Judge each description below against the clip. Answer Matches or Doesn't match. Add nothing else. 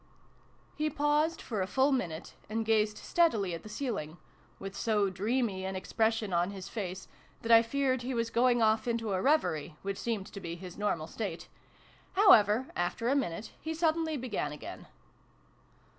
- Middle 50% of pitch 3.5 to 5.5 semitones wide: Matches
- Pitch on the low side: Doesn't match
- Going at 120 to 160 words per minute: Doesn't match